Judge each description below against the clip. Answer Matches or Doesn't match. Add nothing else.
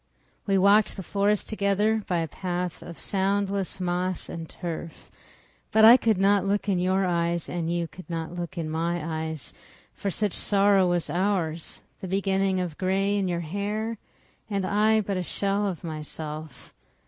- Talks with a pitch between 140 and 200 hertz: Matches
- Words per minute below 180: Matches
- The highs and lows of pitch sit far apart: Doesn't match